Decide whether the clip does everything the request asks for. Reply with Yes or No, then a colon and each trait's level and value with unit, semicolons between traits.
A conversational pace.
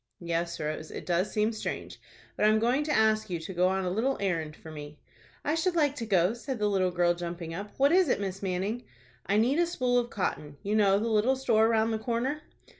No: fast, 240 wpm